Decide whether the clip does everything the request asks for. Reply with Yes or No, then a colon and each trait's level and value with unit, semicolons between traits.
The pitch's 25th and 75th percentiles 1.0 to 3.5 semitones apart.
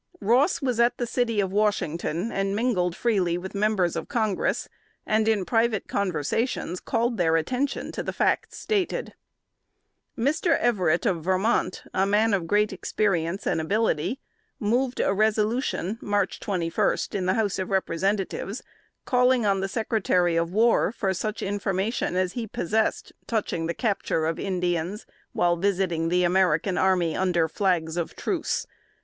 No: average, 3.9 semitones